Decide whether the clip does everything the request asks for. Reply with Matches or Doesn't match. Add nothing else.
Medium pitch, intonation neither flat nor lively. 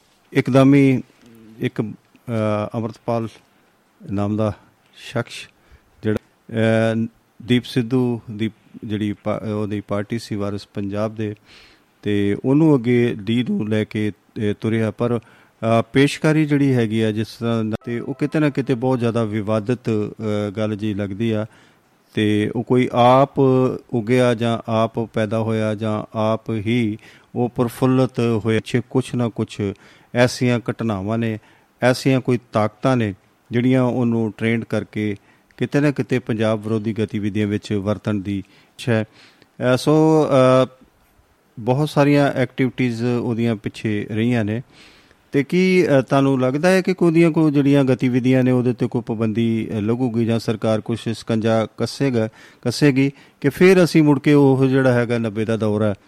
Doesn't match